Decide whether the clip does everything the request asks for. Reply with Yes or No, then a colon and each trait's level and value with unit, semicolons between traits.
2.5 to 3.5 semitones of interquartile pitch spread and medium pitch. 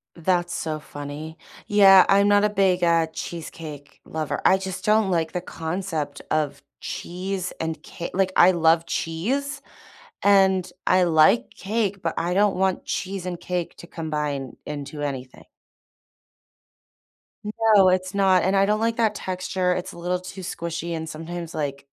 Yes: average, 3.1 semitones; medium, 180 Hz